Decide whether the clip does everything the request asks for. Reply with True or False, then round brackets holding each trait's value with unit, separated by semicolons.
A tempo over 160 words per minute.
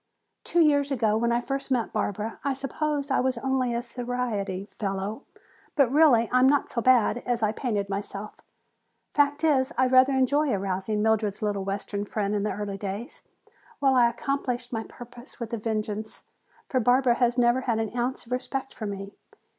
True (185 wpm)